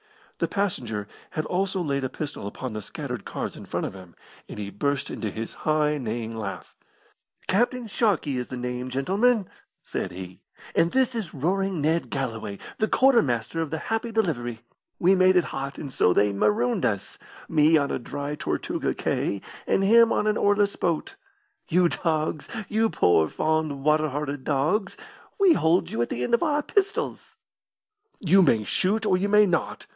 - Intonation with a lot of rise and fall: Yes, wide, 8.0 semitones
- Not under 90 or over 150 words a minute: No, average, 175 wpm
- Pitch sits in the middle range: Yes, medium, 155 Hz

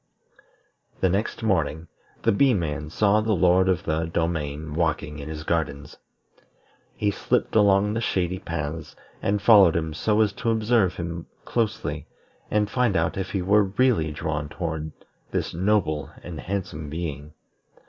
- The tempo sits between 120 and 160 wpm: Yes, average, 150 wpm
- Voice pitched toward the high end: No, very low, 85 Hz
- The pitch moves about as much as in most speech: Yes, average, 4.6 semitones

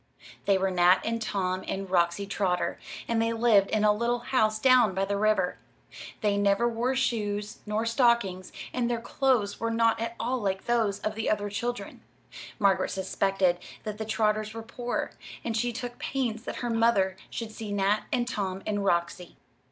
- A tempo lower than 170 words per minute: No, average, 180 wpm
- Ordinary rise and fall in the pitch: Yes, average, 3.1 semitones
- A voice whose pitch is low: No, high, 215 Hz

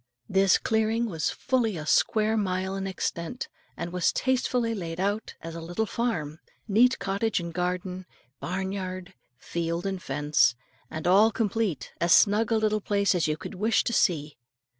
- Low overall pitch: No, high, 190 Hz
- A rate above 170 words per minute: No, average, 160 wpm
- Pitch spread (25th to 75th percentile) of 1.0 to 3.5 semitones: No, average, 4.2 semitones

